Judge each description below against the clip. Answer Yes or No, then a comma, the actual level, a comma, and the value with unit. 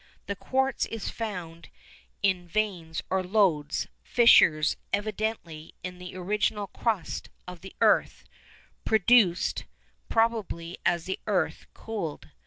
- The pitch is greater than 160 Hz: Yes, high, 190 Hz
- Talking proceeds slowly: Yes, slow, 110 wpm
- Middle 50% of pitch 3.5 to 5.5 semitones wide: Yes, average, 4.0 semitones